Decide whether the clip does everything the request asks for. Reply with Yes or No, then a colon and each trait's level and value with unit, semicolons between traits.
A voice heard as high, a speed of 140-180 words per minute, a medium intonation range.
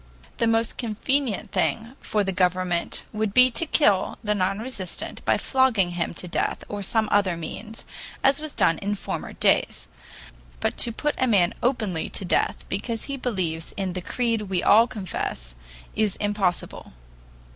Yes: high, 205 Hz; average, 165 wpm; average, 4.1 semitones